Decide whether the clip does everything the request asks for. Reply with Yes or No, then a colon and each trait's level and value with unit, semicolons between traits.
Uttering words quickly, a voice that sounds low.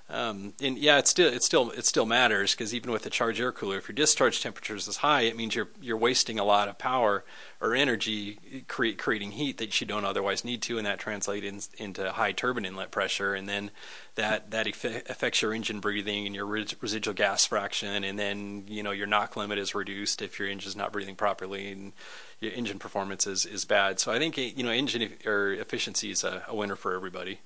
Yes: fast, 230 wpm; low, 105 Hz